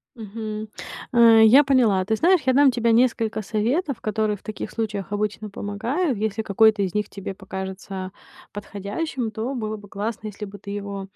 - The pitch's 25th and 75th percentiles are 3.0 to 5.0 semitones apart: No, narrow, 2.4 semitones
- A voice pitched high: Yes, high, 215 Hz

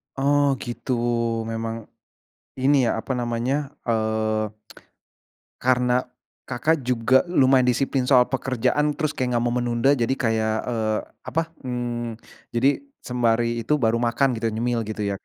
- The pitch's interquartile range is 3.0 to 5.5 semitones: No, narrow, 2.4 semitones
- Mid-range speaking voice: No, low, 120 Hz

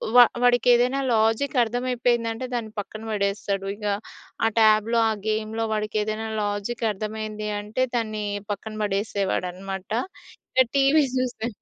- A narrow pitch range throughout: Yes, narrow, 2.3 semitones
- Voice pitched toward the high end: Yes, high, 220 Hz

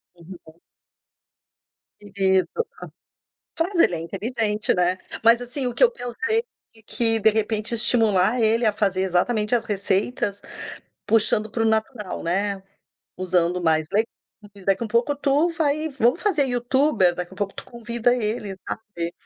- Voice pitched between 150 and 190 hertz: No, high, 215 Hz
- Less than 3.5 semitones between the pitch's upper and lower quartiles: No, average, 4.1 semitones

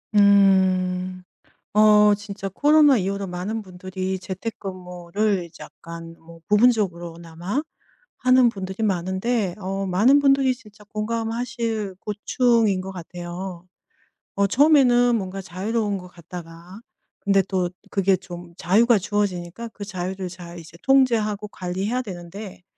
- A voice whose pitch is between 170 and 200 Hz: Yes, high, 195 Hz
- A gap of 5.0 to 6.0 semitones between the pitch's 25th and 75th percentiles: No, average, 3.3 semitones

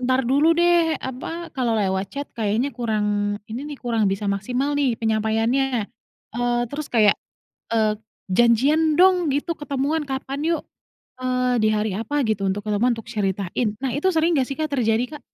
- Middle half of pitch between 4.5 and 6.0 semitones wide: Yes, average, 4.8 semitones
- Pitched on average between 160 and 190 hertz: No, high, 245 Hz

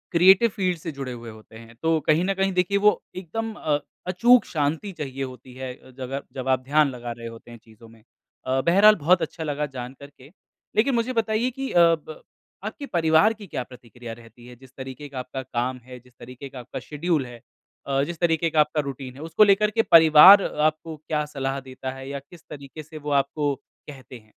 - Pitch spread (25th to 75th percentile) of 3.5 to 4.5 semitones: No, wide, 5.4 semitones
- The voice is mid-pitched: Yes, medium, 145 Hz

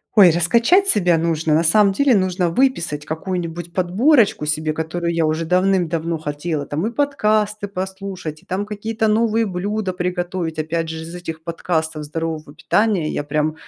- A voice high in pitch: No, medium, 175 Hz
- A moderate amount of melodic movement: Yes, average, 4.1 semitones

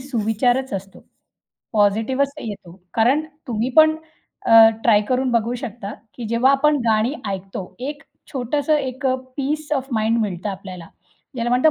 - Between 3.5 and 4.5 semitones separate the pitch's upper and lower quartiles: Yes, average, 3.9 semitones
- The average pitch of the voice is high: Yes, high, 240 Hz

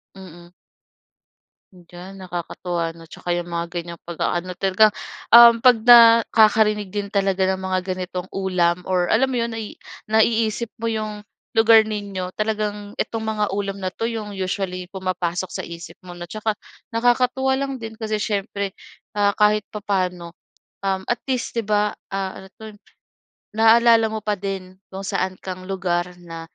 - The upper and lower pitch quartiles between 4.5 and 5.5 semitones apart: No, average, 3.2 semitones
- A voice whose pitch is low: No, high, 200 Hz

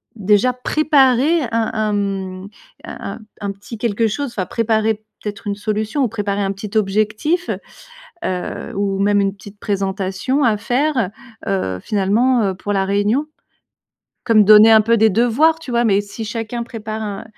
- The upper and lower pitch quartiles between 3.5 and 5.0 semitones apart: No, average, 2.9 semitones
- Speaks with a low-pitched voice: No, high, 215 Hz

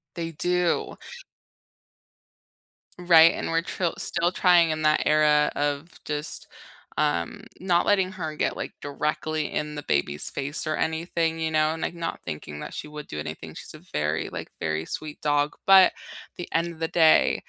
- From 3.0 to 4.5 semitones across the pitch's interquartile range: No, narrow, 2.4 semitones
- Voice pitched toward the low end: No, medium, 155 Hz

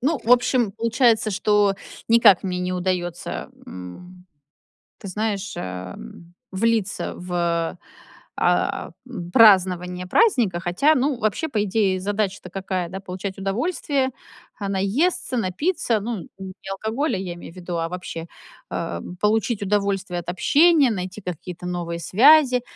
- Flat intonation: No, average, 4.3 semitones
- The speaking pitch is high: Yes, high, 195 Hz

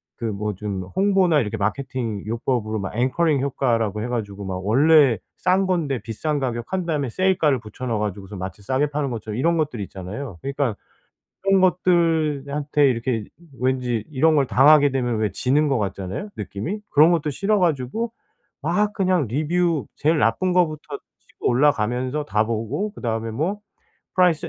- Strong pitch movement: Yes, wide, 6.2 semitones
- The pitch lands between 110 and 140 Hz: Yes, low, 135 Hz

